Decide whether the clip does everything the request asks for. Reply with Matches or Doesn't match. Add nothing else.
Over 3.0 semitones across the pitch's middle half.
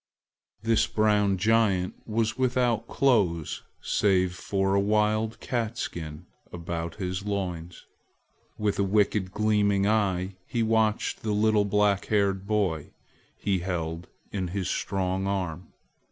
Doesn't match